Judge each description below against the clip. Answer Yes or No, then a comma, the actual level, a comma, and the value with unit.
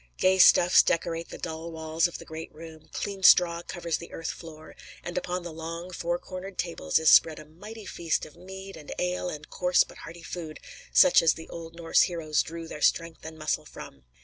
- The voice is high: No, medium, 165 Hz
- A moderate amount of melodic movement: No, narrow, 2.0 semitones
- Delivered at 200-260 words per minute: Yes, fast, 205 wpm